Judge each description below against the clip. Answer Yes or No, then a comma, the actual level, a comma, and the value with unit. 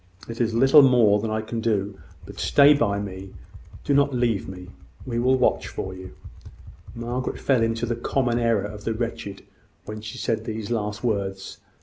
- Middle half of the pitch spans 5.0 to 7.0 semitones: No, average, 2.8 semitones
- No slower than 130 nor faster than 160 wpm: No, average, 170 wpm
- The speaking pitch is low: Yes, low, 115 Hz